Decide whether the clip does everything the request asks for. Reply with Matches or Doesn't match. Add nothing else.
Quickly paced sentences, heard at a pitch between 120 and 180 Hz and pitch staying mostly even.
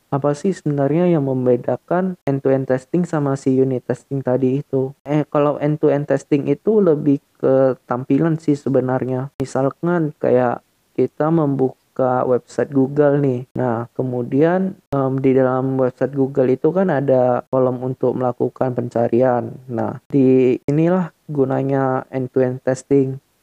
Doesn't match